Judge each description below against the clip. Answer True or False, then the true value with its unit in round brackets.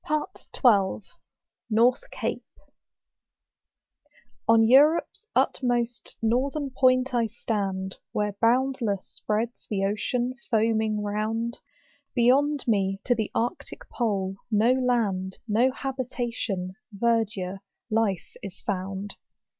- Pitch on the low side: False (225 Hz)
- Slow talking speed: True (95 wpm)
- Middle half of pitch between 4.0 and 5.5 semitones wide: False (3.6 semitones)